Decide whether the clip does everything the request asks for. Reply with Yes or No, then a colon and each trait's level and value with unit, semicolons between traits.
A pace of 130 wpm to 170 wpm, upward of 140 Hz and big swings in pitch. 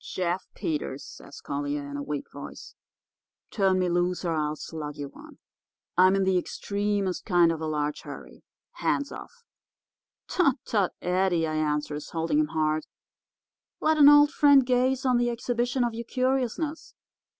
Yes: average, 160 wpm; medium, 185 Hz; wide, 8.1 semitones